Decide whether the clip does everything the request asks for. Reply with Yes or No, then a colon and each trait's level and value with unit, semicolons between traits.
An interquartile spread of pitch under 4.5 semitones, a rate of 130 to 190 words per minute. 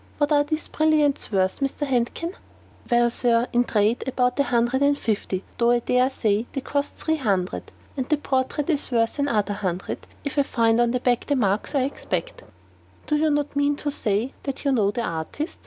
No: average, 4.0 semitones; fast, 205 wpm